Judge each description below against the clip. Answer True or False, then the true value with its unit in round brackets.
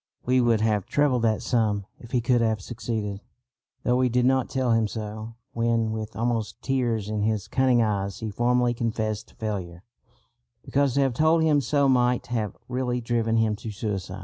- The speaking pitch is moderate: False (115 Hz)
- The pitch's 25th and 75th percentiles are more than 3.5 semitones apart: False (2.4 semitones)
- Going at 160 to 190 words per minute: True (180 wpm)